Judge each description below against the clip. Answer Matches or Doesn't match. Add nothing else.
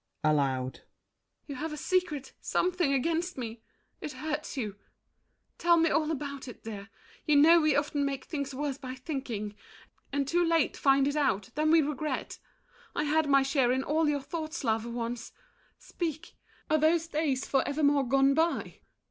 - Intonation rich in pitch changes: Doesn't match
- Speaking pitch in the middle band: Doesn't match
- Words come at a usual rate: Matches